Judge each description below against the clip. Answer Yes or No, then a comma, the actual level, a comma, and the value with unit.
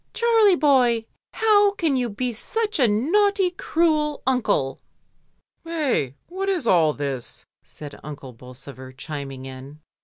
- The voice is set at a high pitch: Yes, very high, 250 Hz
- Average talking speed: No, slow, 125 wpm